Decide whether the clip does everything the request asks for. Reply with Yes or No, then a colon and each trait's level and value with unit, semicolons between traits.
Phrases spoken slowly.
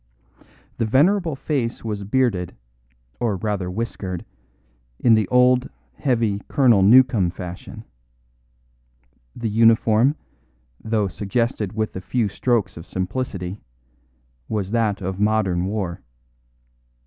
Yes: slow, 105 wpm